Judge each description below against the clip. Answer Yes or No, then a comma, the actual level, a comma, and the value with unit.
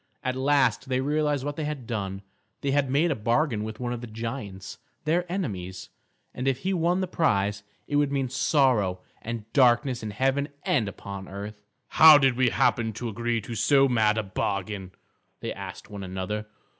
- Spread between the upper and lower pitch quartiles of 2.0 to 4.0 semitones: No, average, 5.1 semitones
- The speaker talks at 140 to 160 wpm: No, average, 185 wpm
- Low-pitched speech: Yes, low, 120 Hz